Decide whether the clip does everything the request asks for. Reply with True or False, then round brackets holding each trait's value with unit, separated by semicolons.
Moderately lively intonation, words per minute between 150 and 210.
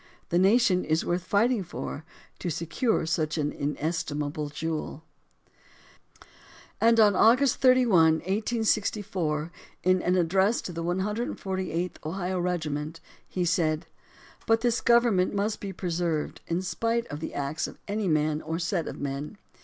False (4.7 semitones; 140 wpm)